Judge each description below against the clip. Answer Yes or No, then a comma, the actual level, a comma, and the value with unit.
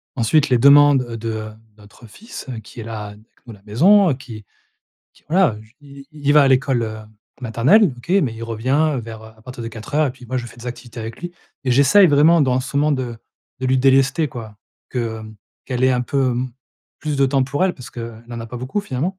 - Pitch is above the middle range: No, low, 130 Hz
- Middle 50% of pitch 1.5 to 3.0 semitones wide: No, average, 3.8 semitones